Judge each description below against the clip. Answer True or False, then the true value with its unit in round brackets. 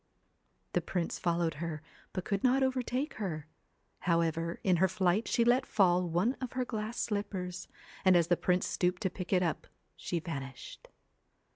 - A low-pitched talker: False (180 Hz)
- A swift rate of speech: False (165 wpm)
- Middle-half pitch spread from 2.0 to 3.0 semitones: False (4.0 semitones)